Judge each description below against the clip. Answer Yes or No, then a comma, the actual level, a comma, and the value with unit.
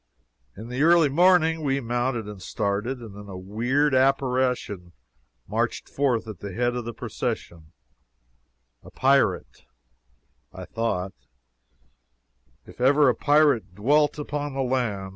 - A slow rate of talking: Yes, slow, 125 wpm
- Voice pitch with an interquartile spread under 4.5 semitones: No, average, 5.3 semitones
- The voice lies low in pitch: Yes, low, 125 Hz